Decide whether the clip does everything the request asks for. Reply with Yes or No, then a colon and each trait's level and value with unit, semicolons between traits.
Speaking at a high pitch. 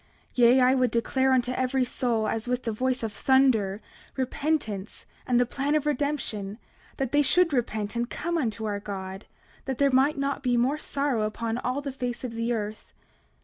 Yes: very high, 250 Hz